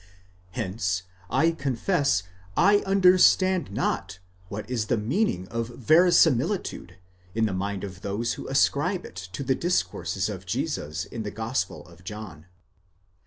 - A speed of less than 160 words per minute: Yes, average, 140 wpm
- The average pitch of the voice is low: Yes, low, 110 Hz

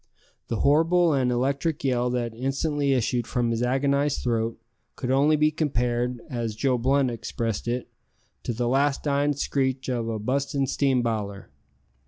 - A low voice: Yes, low, 130 Hz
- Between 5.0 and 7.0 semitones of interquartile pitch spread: No, average, 2.8 semitones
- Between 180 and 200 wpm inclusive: No, average, 155 wpm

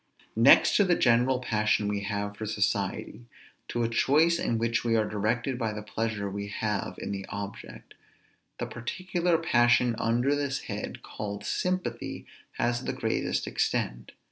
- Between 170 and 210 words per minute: No, average, 155 wpm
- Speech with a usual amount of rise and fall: Yes, average, 3.5 semitones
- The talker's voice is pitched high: No, low, 115 Hz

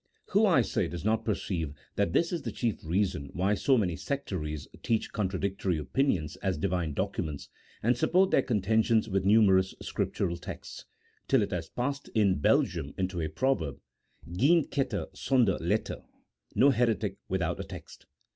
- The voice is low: Yes, low, 100 Hz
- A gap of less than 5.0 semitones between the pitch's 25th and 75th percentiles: No, average, 5.3 semitones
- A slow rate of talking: No, average, 160 wpm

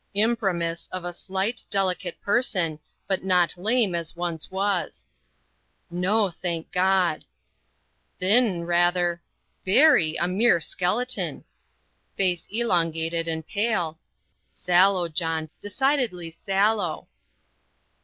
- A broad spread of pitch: No, average, 3.1 semitones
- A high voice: No, medium, 180 Hz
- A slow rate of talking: Yes, slow, 105 wpm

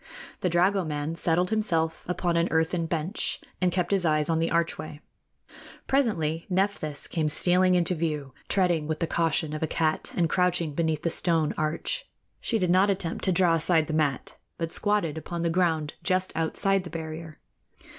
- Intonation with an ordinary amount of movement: No, narrow, 2.3 semitones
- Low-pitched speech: No, medium, 165 Hz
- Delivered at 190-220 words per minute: No, average, 175 wpm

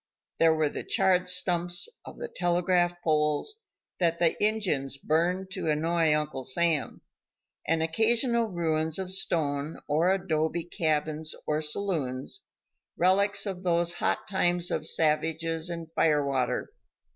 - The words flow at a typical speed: No, slow, 130 wpm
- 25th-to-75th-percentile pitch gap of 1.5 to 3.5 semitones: Yes, average, 2.8 semitones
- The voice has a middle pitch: Yes, medium, 170 Hz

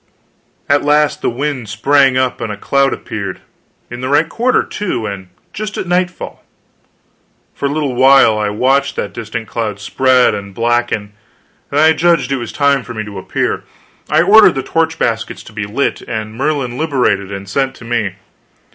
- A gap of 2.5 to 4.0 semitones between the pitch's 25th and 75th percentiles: No, average, 5.0 semitones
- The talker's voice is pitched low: Yes, low, 130 Hz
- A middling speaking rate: Yes, average, 180 wpm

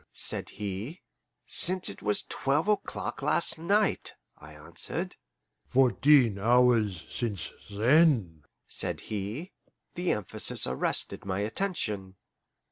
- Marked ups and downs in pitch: Yes, wide, 7.6 semitones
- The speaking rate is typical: No, slow, 105 wpm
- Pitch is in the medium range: No, low, 110 Hz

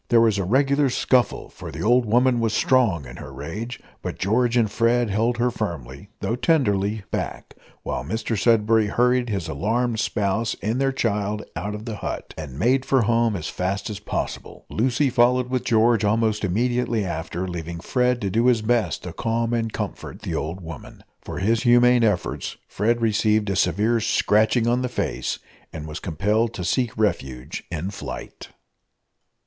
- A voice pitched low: Yes, low, 110 Hz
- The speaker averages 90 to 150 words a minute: No, average, 175 wpm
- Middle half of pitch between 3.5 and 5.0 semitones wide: Yes, average, 3.8 semitones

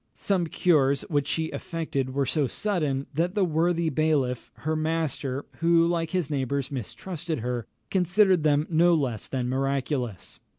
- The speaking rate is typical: Yes, average, 145 wpm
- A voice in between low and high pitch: Yes, medium, 155 Hz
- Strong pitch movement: No, average, 3.8 semitones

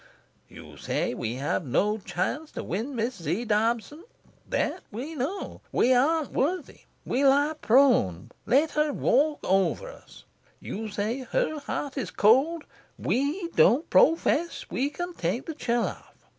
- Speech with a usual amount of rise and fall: No, wide, 6.1 semitones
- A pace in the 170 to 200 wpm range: No, average, 150 wpm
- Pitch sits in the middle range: No, very high, 265 Hz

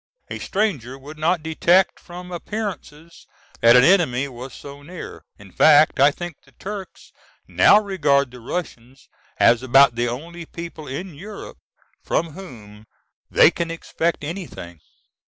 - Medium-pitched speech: Yes, medium, 155 Hz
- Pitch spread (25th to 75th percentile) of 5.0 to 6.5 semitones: Yes, average, 5.3 semitones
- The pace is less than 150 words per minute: Yes, average, 140 wpm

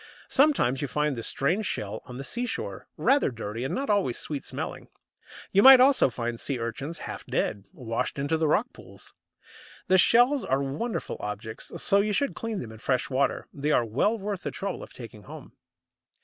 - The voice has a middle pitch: Yes, medium, 145 Hz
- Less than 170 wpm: No, average, 190 wpm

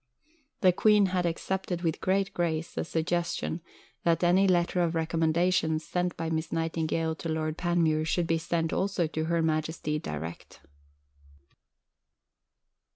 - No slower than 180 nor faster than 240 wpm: No, average, 140 wpm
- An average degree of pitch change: No, narrow, 1.9 semitones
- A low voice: No, medium, 165 Hz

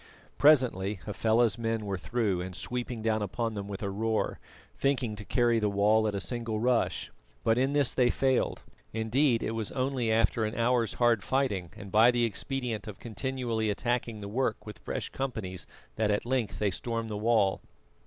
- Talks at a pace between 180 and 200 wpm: Yes, average, 185 wpm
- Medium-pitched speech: No, low, 115 Hz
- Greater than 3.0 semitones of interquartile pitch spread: No, average, 2.7 semitones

